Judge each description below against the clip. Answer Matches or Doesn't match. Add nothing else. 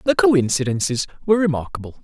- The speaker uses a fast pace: Doesn't match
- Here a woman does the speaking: Doesn't match